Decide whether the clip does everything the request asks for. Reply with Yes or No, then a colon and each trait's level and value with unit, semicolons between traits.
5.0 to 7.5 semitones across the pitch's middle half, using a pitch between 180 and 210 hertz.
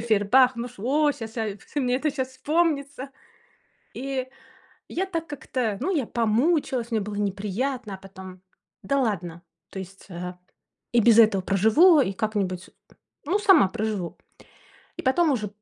No: wide, 5.6 semitones; high, 235 Hz